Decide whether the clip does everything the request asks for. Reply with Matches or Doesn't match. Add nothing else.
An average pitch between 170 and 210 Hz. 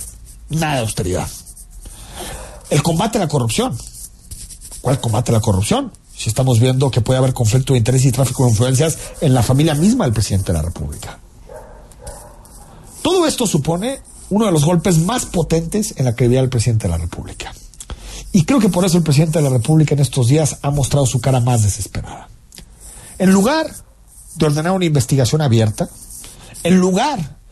Doesn't match